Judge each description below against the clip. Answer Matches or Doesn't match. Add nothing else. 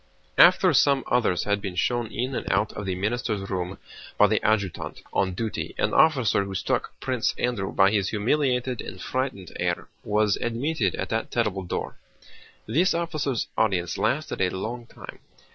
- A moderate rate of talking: Matches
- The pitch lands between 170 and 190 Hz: Doesn't match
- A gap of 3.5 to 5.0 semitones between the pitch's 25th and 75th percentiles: Matches